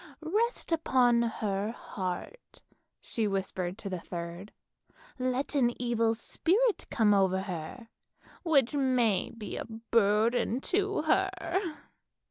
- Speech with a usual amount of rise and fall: No, wide, 6.2 semitones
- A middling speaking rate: No, slow, 115 wpm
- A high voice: Yes, high, 230 Hz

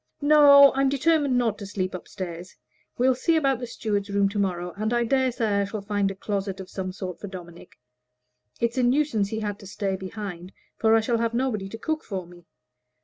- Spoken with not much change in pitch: No, average, 4.4 semitones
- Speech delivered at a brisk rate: Yes, fast, 215 wpm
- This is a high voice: Yes, high, 210 Hz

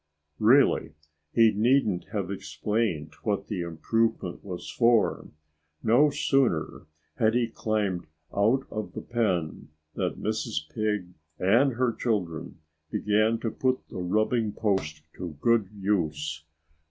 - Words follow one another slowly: Yes, slow, 120 wpm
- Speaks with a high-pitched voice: No, low, 105 Hz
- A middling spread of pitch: Yes, average, 4.6 semitones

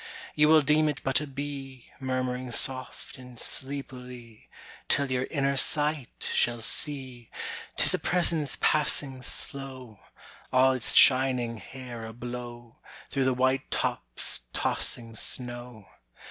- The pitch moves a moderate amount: No, narrow, 2.3 semitones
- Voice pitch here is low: Yes, low, 130 Hz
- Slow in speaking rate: Yes, slow, 120 wpm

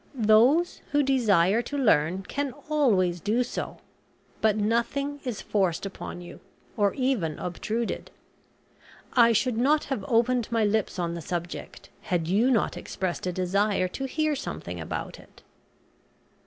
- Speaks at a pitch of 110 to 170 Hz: No, high, 220 Hz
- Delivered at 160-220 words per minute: No, average, 140 wpm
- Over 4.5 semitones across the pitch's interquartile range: Yes, wide, 5.6 semitones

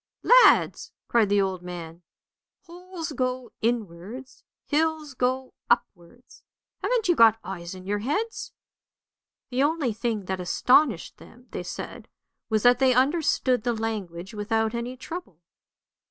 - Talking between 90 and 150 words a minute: Yes, slow, 135 wpm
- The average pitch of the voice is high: Yes, high, 240 Hz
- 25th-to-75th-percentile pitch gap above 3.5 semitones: Yes, wide, 5.6 semitones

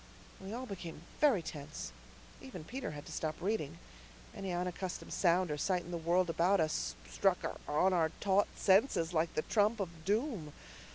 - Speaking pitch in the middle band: Yes, medium, 175 Hz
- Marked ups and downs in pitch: No, average, 3.8 semitones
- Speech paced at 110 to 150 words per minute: No, average, 170 wpm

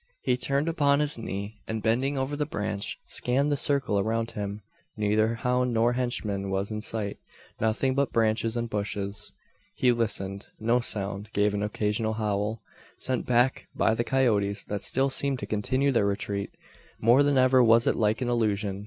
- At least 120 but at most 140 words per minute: No, average, 175 wpm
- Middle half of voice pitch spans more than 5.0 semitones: No, average, 3.7 semitones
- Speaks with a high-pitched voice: No, low, 115 Hz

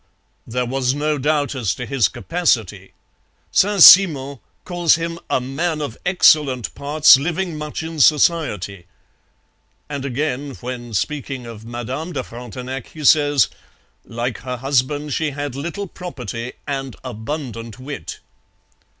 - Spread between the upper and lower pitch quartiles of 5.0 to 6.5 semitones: No, average, 3.8 semitones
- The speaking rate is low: Yes, slow, 130 wpm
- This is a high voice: No, medium, 140 Hz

